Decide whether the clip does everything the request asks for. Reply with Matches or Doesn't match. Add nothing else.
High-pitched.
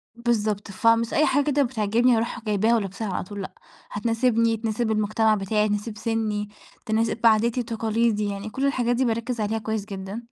Matches